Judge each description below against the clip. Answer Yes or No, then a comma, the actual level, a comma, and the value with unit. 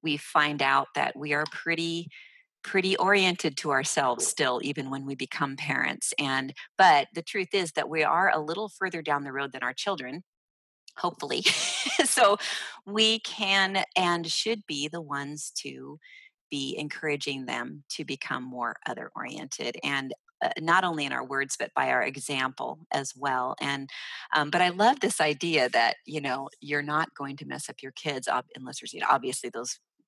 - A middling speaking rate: Yes, average, 180 wpm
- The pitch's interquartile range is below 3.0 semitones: No, average, 4.5 semitones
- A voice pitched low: No, medium, 150 Hz